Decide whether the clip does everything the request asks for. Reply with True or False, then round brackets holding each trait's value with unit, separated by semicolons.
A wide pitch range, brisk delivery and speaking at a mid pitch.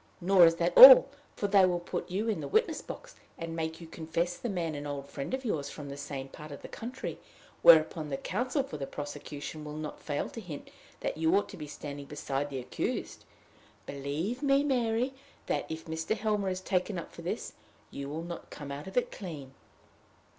True (5.8 semitones; 210 wpm; 165 Hz)